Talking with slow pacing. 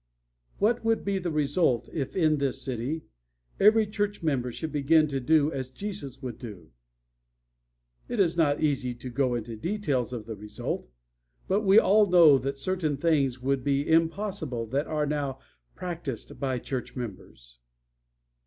No: average, 155 wpm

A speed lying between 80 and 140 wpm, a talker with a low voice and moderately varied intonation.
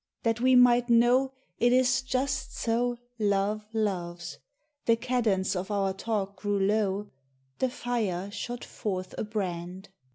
No: slow, 135 wpm; high, 215 Hz; average, 3.9 semitones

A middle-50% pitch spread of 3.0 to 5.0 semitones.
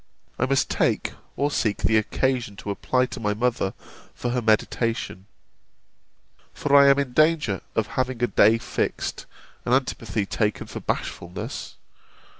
Yes: average, 3.6 semitones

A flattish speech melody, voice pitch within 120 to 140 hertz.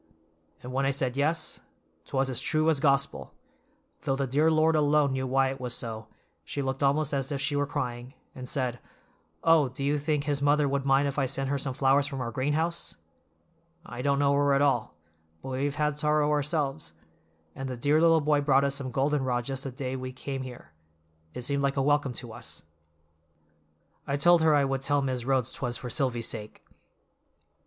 Yes: narrow, 2.1 semitones; low, 135 Hz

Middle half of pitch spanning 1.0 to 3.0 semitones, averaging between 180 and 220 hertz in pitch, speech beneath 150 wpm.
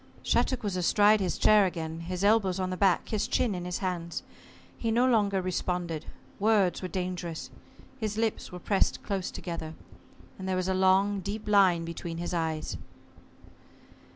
No: average, 2.7 semitones; medium, 185 Hz; average, 165 wpm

